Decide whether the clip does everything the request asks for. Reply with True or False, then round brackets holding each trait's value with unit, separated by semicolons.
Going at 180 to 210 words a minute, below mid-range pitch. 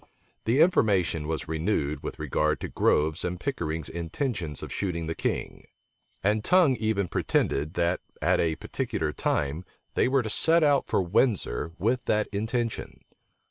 False (150 wpm; 95 Hz)